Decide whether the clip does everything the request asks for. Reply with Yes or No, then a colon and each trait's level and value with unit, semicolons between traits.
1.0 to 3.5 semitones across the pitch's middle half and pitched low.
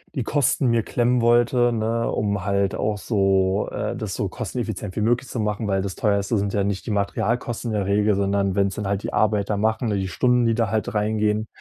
Yes: narrow, 2.6 semitones; low, 105 Hz